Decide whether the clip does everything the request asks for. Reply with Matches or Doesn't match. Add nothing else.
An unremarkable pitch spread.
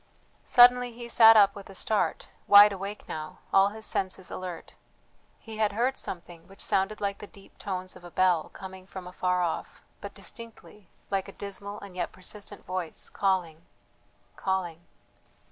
Doesn't match